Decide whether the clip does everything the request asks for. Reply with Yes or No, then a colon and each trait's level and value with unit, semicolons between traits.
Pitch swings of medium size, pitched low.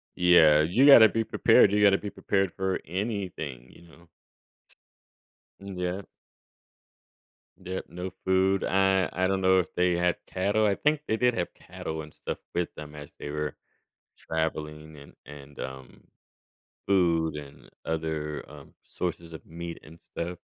Yes: average, 3.6 semitones; very low, 90 Hz